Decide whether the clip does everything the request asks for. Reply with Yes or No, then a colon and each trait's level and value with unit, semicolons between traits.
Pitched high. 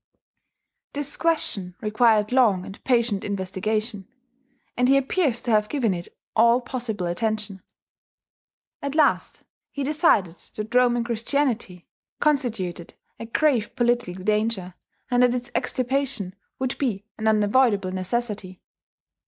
Yes: high, 230 Hz